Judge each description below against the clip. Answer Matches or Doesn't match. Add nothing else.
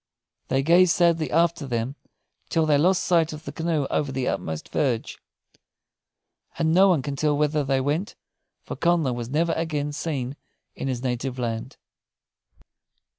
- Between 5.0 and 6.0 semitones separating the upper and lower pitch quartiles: Doesn't match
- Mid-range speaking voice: Matches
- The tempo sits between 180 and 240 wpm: Doesn't match